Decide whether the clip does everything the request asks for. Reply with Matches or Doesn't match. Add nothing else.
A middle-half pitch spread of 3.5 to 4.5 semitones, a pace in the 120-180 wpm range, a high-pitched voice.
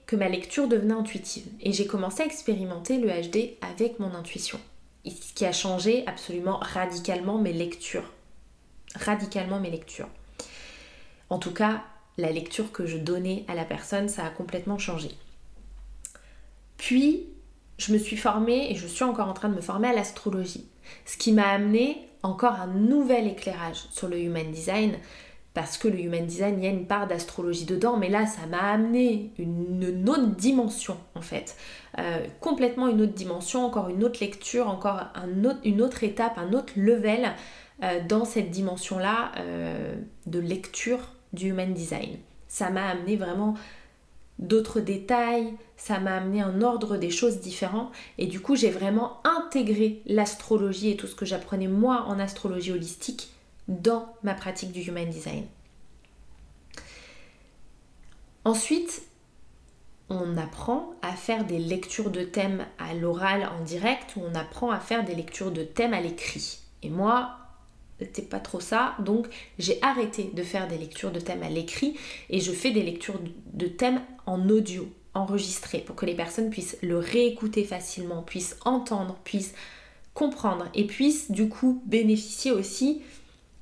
Matches